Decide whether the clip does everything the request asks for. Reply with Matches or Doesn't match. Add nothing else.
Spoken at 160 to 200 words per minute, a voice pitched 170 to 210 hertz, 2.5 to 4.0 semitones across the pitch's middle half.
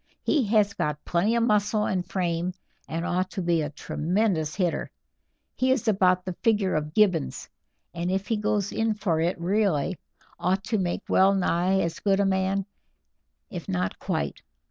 Matches